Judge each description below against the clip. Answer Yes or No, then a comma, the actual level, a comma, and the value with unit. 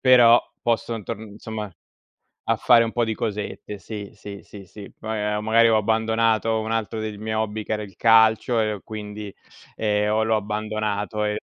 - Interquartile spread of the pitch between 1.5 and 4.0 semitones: No, narrow, 1.1 semitones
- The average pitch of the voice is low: Yes, low, 110 Hz